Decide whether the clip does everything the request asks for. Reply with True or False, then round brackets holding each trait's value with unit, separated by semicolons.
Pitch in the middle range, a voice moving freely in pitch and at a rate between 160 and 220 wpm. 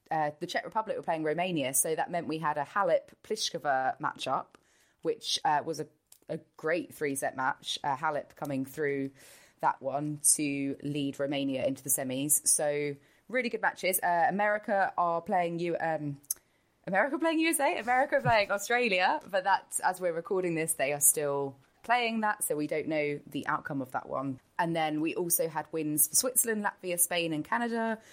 True (165 Hz; 6.2 semitones; 175 wpm)